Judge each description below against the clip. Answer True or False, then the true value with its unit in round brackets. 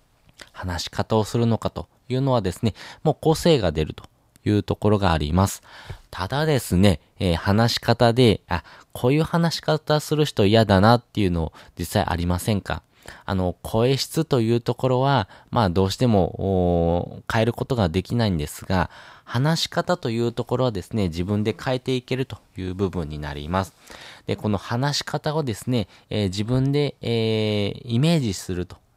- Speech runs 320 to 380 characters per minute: True (330 characters per minute)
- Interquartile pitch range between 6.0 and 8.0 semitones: False (5.3 semitones)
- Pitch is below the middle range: True (110 Hz)